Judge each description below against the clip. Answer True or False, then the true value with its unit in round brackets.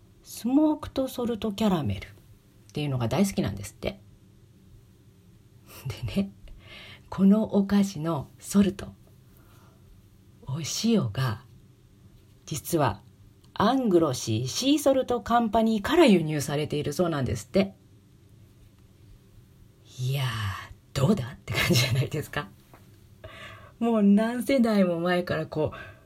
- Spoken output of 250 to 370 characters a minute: False (240 characters per minute)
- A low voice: True (130 Hz)